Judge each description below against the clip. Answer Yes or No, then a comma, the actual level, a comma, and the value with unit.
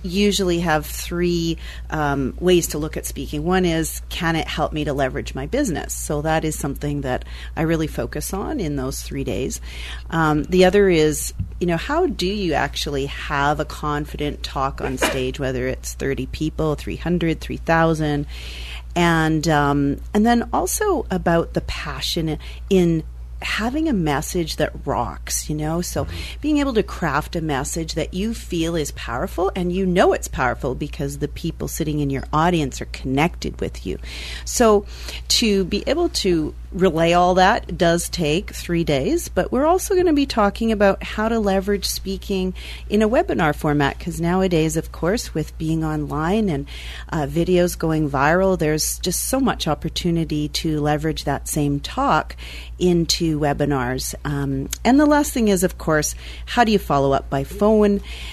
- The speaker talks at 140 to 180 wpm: Yes, average, 170 wpm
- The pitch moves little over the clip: No, average, 4.4 semitones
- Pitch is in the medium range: Yes, medium, 160 Hz